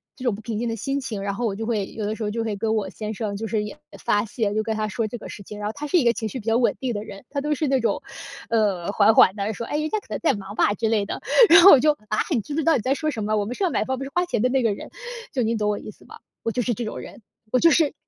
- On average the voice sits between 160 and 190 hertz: No, high, 225 Hz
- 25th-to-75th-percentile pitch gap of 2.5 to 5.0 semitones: Yes, average, 3.8 semitones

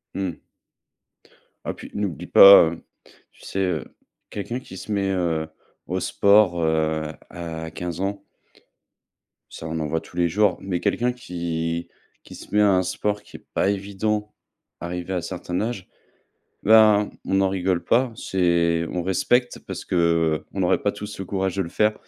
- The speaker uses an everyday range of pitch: Yes, average, 3.2 semitones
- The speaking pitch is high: No, very low, 95 Hz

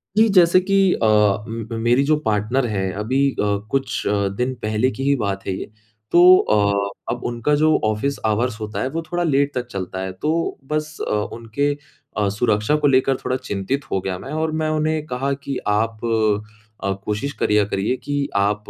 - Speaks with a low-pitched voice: Yes, low, 120 Hz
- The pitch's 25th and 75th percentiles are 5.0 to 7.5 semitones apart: Yes, average, 5.3 semitones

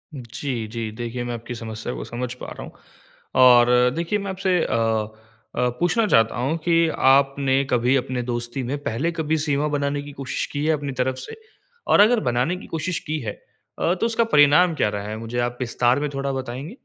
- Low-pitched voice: Yes, low, 130 Hz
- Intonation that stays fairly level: No, average, 4.2 semitones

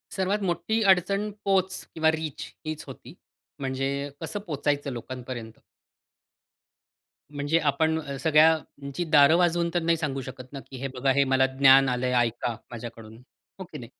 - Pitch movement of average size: Yes, average, 3.7 semitones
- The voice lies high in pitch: No, medium, 140 Hz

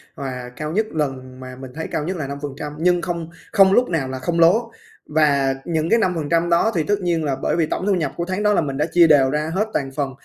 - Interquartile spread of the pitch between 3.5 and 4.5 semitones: Yes, average, 4.1 semitones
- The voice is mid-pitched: Yes, medium, 155 Hz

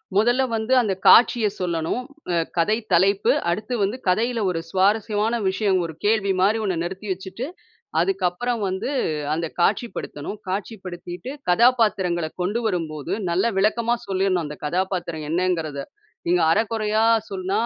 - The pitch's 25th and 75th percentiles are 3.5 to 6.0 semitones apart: Yes, average, 3.9 semitones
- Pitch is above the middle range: Yes, high, 195 Hz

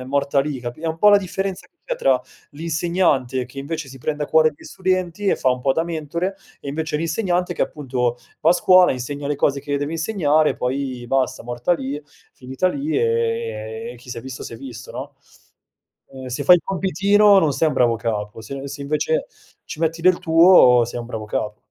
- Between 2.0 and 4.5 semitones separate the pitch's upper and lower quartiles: No, average, 5.1 semitones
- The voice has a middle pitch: Yes, medium, 145 Hz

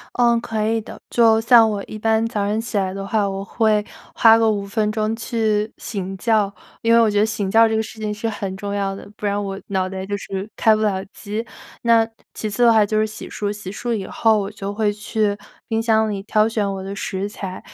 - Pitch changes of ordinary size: No, narrow, 1.8 semitones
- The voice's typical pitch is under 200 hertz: No, high, 210 Hz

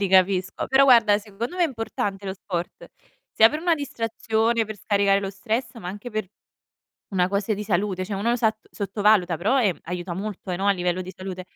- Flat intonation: No, average, 3.1 semitones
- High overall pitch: Yes, high, 200 Hz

